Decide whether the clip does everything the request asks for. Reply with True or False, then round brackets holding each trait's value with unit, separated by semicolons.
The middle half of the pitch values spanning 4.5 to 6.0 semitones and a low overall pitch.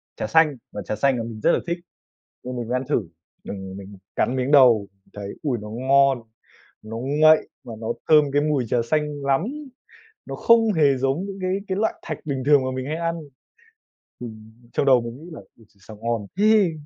True (5.2 semitones; 130 Hz)